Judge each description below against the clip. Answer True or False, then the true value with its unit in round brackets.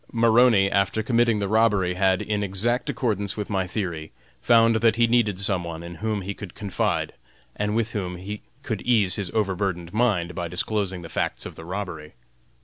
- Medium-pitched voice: False (100 Hz)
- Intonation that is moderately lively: True (3.5 semitones)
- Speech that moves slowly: False (185 wpm)